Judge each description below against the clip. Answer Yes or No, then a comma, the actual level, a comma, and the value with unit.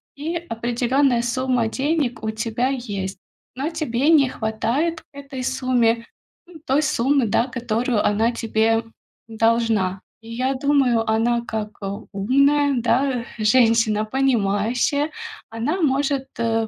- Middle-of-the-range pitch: No, high, 240 Hz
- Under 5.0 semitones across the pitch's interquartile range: Yes, average, 3.4 semitones